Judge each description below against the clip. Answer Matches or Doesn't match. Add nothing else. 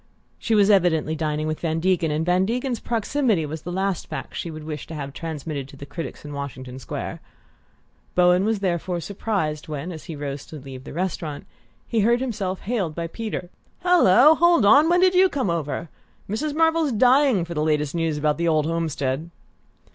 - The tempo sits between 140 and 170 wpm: Doesn't match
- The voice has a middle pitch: Matches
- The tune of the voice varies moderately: Doesn't match